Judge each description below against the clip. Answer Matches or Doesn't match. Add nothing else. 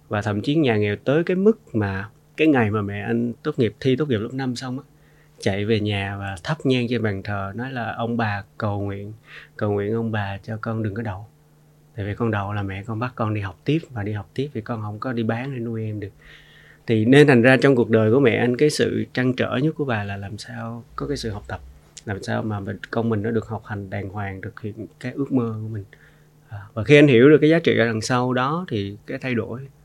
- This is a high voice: Doesn't match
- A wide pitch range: Doesn't match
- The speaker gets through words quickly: Matches